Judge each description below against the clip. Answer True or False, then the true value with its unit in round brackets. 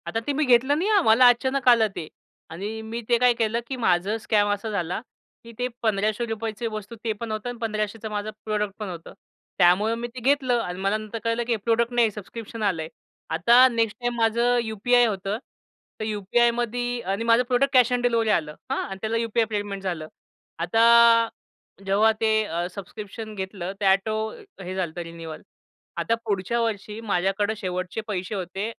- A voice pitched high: True (220 Hz)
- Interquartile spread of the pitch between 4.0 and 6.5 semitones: False (3.0 semitones)